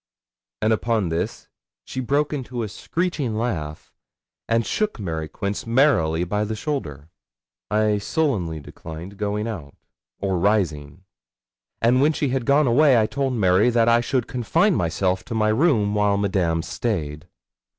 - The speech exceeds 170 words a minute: No, average, 150 wpm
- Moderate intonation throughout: No, wide, 5.8 semitones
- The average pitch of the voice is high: No, low, 110 Hz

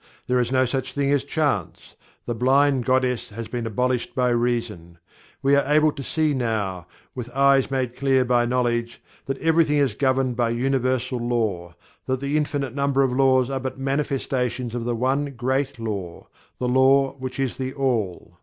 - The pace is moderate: Yes, average, 175 wpm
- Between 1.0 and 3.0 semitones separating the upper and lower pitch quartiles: Yes, narrow, 2.4 semitones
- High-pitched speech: No, low, 130 Hz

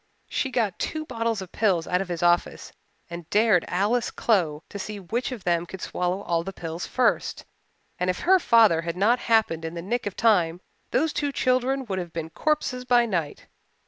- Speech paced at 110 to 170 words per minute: No, average, 200 wpm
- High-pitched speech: Yes, high, 195 Hz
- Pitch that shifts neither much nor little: No, wide, 5.7 semitones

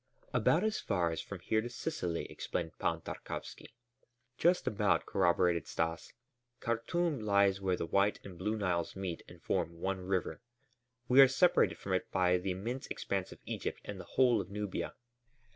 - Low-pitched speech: Yes, very low, 95 Hz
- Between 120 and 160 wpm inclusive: No, average, 170 wpm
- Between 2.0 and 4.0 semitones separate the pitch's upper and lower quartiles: No, average, 4.4 semitones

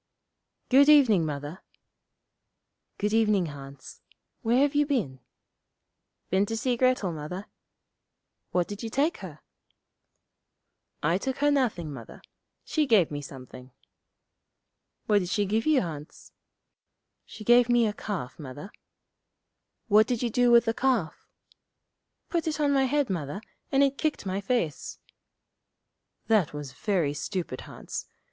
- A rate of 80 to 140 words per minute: Yes, slow, 135 wpm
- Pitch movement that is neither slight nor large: No, wide, 8.1 semitones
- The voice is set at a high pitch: Yes, high, 210 Hz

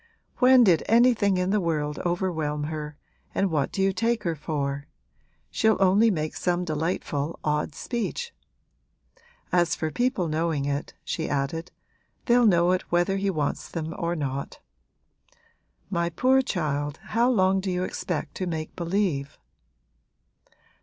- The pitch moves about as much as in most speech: Yes, average, 4.3 semitones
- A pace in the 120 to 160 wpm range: Yes, average, 140 wpm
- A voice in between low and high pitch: Yes, medium, 175 Hz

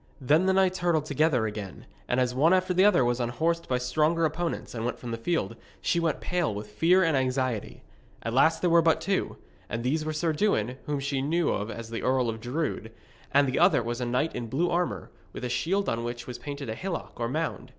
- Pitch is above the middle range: No, medium, 140 Hz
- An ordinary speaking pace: No, fast, 230 wpm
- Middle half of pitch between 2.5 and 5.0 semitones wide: No, wide, 5.6 semitones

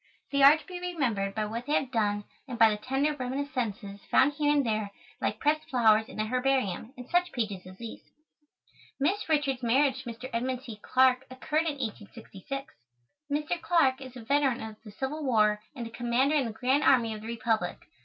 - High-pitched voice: Yes, very high, 255 Hz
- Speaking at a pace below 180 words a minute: No, average, 200 wpm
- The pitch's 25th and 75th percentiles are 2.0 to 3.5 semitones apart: No, average, 4.2 semitones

